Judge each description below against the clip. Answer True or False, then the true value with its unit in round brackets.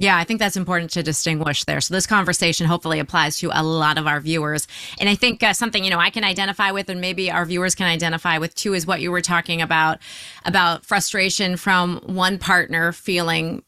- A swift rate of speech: True (220 wpm)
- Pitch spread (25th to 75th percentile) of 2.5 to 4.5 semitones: True (2.8 semitones)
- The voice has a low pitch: False (175 Hz)